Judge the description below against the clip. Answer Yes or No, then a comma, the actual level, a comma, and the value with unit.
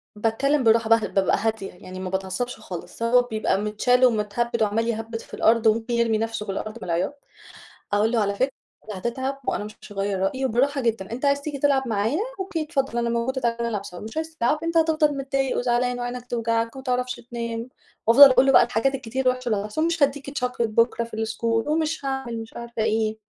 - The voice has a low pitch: No, high, 235 Hz